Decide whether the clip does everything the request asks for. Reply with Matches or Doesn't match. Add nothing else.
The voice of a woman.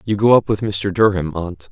Doesn't match